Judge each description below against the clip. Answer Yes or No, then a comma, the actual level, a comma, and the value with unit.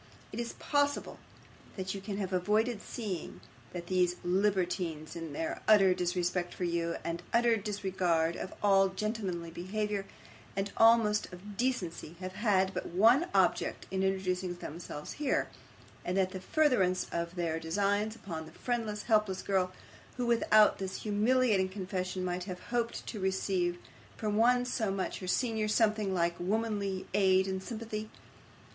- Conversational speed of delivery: Yes, average, 150 wpm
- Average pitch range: Yes, average, 3.0 semitones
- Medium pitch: No, high, 195 Hz